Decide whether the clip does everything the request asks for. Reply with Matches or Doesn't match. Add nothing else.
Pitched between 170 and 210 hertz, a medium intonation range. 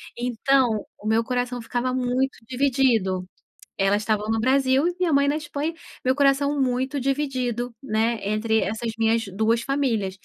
Doesn't match